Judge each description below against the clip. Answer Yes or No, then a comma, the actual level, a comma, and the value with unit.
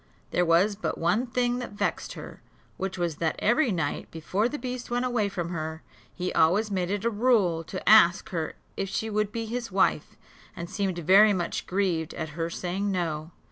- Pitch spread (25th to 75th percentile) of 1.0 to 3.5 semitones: No, average, 4.3 semitones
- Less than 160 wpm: No, average, 195 wpm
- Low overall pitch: No, high, 195 Hz